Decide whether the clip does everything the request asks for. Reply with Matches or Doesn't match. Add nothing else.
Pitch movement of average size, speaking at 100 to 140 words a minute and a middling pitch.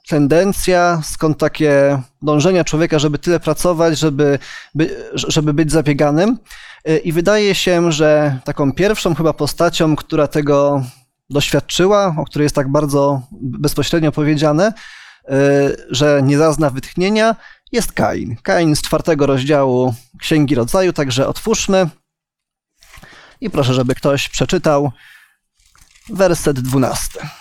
Matches